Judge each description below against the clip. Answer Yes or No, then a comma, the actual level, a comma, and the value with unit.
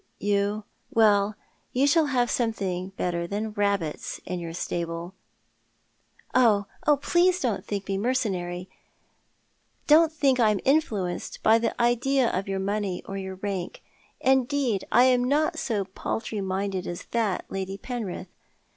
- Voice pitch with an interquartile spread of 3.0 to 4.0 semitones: No, average, 4.7 semitones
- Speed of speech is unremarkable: Yes, average, 145 wpm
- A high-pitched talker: Yes, high, 205 Hz